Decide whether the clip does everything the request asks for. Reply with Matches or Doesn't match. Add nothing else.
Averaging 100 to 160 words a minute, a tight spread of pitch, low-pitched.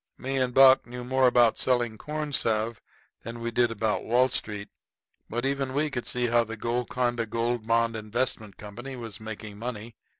Doesn't match